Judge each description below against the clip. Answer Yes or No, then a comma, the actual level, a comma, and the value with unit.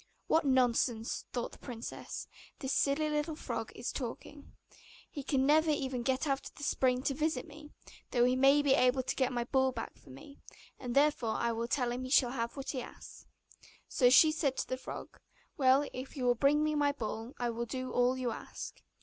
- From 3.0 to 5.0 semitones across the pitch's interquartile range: No, narrow, 2.6 semitones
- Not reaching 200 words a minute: No, fast, 205 wpm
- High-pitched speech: Yes, very high, 260 Hz